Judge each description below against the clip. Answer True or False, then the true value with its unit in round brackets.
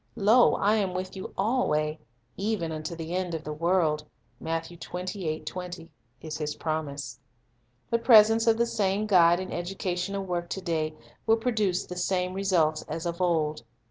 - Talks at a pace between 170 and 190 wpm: False (155 wpm)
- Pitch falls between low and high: True (180 Hz)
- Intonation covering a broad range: False (3.7 semitones)